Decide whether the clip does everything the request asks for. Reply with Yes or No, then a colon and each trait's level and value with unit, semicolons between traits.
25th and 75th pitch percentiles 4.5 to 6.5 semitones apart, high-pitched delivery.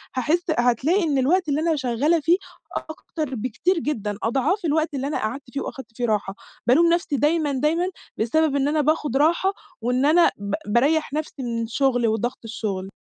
Yes: average, 4.8 semitones; very high, 280 Hz